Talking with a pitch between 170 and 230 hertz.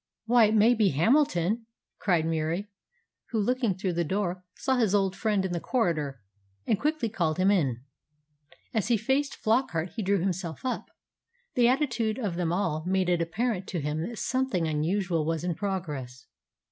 Yes: high, 190 Hz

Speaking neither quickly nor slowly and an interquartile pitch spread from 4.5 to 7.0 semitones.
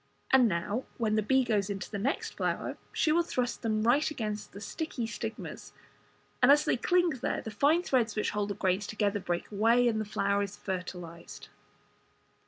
No: average, 190 wpm; average, 3.8 semitones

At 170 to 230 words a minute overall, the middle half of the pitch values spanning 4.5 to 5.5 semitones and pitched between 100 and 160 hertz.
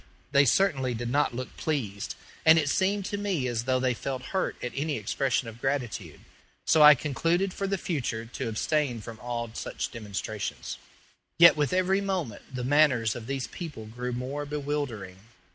Yes: average, 175 wpm; average, 4.8 semitones; low, 135 Hz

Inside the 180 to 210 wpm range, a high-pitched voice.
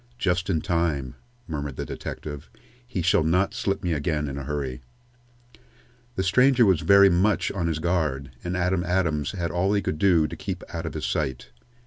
No: average, 185 wpm; very low, 85 Hz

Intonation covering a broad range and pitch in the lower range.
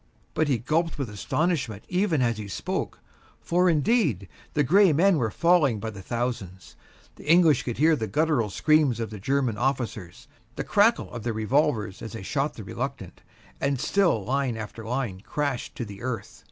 Yes: wide, 6.1 semitones; low, 130 Hz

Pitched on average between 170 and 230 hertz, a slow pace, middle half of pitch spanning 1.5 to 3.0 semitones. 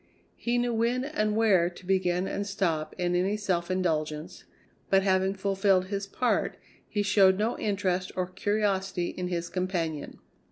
No: high, 190 Hz; average, 155 wpm; narrow, 2.4 semitones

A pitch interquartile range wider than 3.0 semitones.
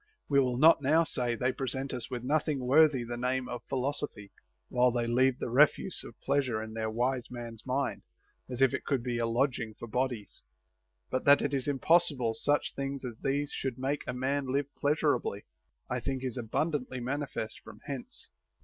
No: average, 2.7 semitones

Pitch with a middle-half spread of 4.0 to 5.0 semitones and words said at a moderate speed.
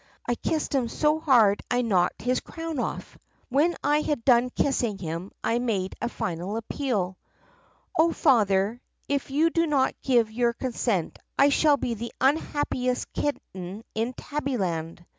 No: wide, 5.6 semitones; average, 155 wpm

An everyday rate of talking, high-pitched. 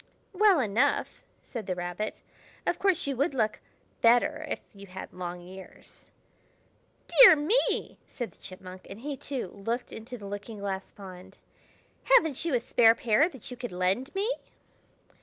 Yes: average, 160 wpm; high, 225 Hz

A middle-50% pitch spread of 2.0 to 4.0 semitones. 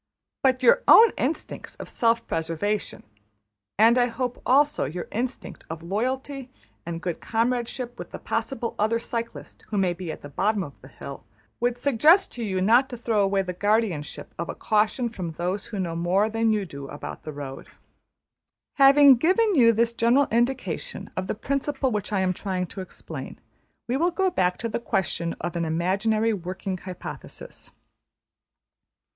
No: average, 5.3 semitones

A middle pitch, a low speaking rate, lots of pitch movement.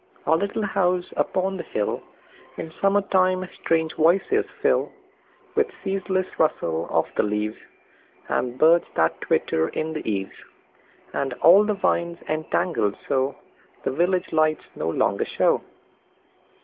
Yes: medium, 165 Hz; slow, 115 wpm; wide, 5.9 semitones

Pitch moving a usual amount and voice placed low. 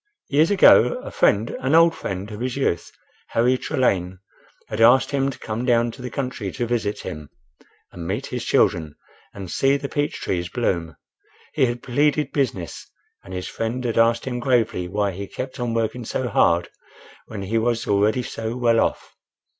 Yes: average, 4.4 semitones; low, 115 Hz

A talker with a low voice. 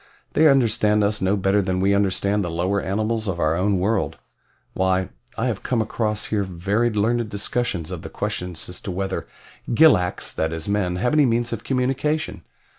Yes: low, 100 Hz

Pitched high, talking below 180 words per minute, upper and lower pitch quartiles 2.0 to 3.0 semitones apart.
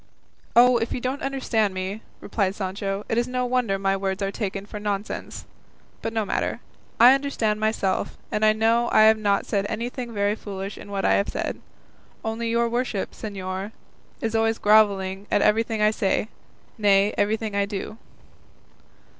Yes: high, 215 Hz; average, 170 wpm; narrow, 2.4 semitones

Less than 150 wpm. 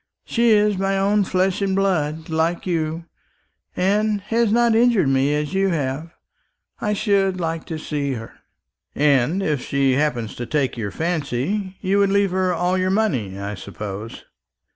No: average, 165 wpm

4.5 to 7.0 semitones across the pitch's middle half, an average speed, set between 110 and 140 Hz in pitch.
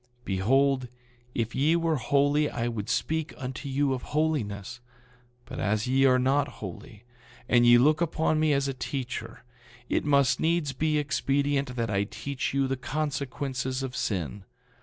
No: average, 3.2 semitones; average, 160 wpm; low, 135 Hz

